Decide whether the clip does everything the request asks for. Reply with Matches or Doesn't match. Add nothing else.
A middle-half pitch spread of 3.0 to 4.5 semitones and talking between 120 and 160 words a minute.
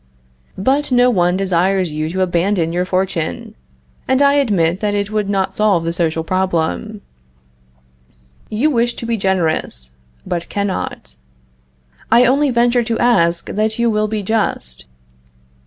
Doesn't match